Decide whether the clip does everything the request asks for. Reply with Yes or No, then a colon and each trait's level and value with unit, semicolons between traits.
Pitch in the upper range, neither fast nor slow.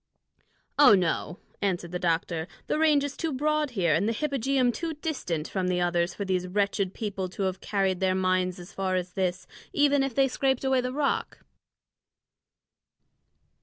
Yes: high, 195 Hz; average, 170 wpm